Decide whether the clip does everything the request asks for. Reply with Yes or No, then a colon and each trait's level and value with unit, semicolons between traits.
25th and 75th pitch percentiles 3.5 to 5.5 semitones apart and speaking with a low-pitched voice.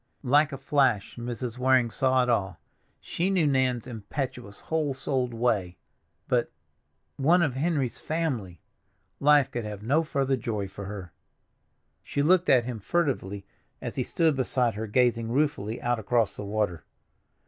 Yes: average, 4.7 semitones; low, 125 Hz